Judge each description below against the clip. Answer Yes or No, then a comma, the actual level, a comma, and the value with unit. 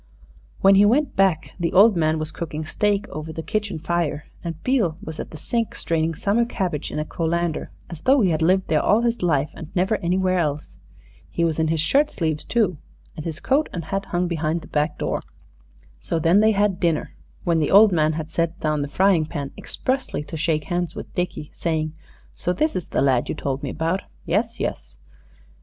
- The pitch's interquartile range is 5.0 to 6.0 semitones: No, average, 3.9 semitones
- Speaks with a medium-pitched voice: Yes, medium, 170 Hz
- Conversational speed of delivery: No, fast, 210 wpm